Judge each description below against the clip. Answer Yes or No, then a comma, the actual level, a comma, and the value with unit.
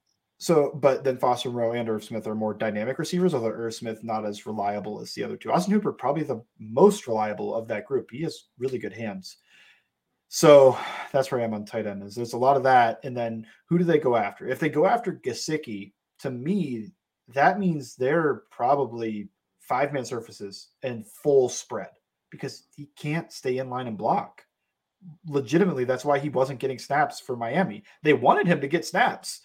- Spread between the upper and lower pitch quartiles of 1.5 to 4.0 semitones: No, average, 4.9 semitones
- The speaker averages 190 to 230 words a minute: Yes, average, 200 wpm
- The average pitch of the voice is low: Yes, low, 130 Hz